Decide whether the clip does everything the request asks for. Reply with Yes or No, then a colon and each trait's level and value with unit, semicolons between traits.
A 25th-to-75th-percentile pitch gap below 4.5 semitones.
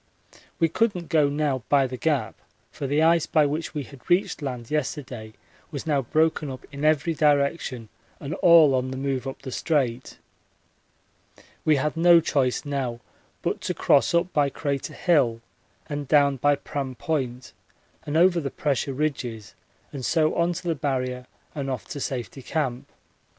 Yes: average, 3.2 semitones